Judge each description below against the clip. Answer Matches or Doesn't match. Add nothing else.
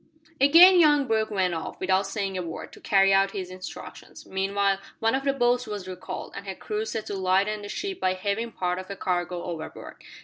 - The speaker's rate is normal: Doesn't match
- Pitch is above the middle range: Matches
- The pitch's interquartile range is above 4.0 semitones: Doesn't match